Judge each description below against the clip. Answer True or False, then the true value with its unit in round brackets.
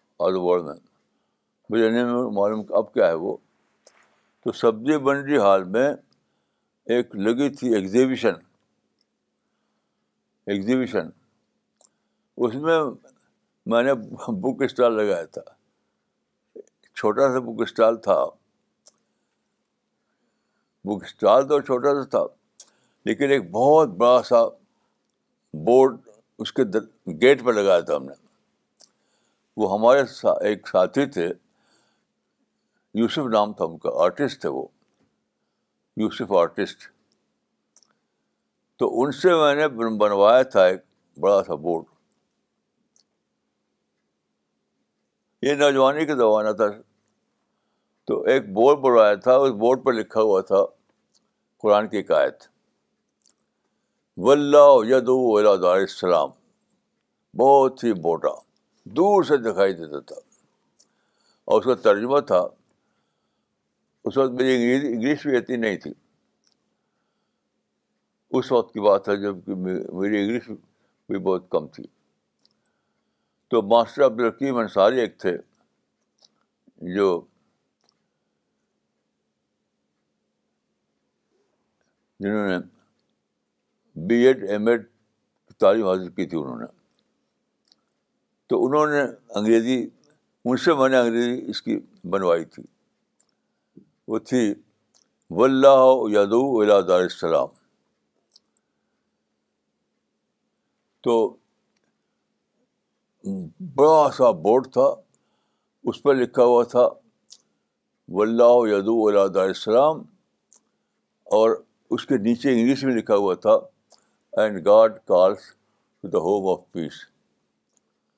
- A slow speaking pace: True (105 wpm)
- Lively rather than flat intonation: False (4.9 semitones)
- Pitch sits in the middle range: False (120 Hz)